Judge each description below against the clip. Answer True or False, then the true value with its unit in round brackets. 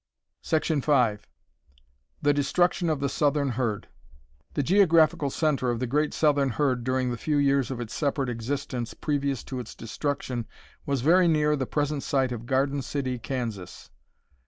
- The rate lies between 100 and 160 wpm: True (155 wpm)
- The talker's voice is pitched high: False (140 Hz)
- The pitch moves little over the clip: False (3.1 semitones)